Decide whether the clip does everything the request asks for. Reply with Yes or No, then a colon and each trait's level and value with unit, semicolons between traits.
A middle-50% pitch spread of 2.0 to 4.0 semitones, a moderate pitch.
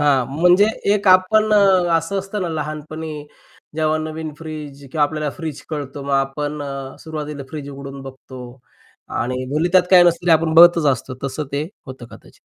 Yes: average, 3.4 semitones; medium, 155 Hz